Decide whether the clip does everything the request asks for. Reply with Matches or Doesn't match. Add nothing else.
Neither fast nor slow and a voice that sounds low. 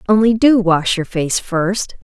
Doesn't match